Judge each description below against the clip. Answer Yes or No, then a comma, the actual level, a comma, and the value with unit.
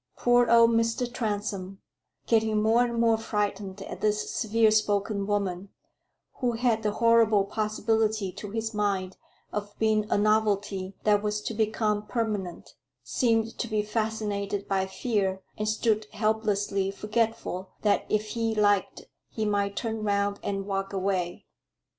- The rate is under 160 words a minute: Yes, average, 140 wpm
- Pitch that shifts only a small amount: Yes, narrow, 1.8 semitones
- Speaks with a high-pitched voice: Yes, high, 210 Hz